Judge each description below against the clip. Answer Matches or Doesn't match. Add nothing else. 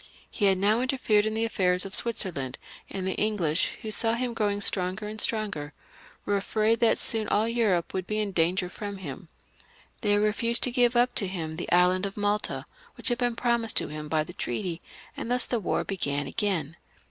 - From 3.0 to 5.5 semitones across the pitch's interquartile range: Matches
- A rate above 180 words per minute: Matches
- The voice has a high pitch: Matches